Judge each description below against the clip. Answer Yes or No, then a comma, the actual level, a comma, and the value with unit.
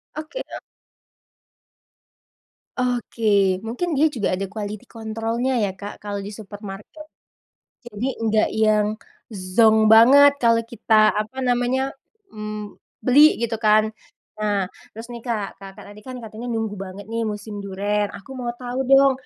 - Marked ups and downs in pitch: No, average, 3.0 semitones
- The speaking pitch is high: Yes, high, 220 Hz